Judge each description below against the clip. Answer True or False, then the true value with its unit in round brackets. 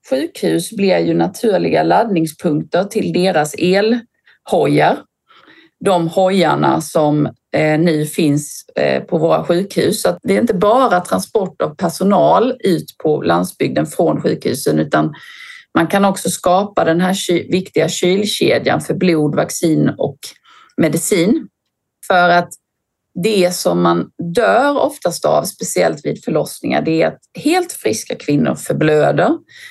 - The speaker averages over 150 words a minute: False (125 wpm)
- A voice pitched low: False (175 Hz)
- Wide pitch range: False (4.8 semitones)